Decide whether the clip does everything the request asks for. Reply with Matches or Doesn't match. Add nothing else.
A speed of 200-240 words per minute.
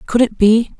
Matches